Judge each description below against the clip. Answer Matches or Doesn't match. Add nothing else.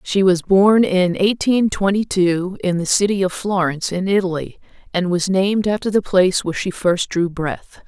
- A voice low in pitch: Doesn't match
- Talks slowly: Doesn't match